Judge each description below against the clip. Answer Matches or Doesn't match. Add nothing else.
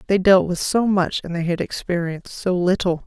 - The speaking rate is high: Matches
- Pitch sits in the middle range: Matches